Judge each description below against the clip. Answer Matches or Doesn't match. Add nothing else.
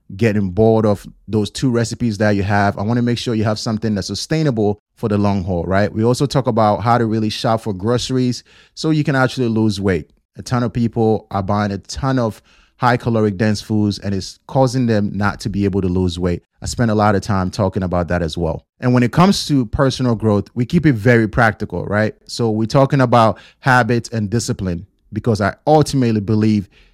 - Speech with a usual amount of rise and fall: Matches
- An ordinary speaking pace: Doesn't match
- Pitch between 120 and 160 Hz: Doesn't match